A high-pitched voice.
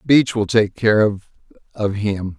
No: low, 105 Hz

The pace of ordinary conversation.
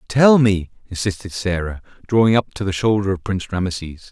Yes: average, 175 wpm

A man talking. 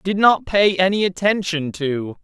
Yes: male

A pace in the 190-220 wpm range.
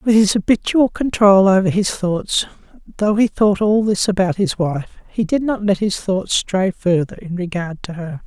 Yes: average, 195 wpm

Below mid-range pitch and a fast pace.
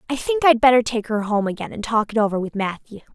No: high, 230 Hz; fast, 265 wpm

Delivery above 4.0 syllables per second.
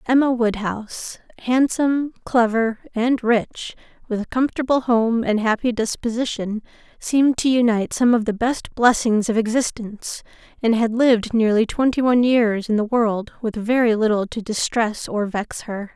Yes: 4.9 syllables/s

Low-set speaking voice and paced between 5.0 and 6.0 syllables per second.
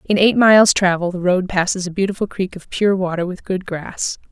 No: medium, 185 Hz; 5.3 syllables/s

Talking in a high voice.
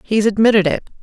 Yes: high, 210 Hz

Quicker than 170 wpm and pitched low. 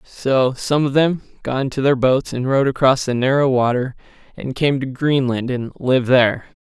Yes: average, 190 wpm; low, 130 Hz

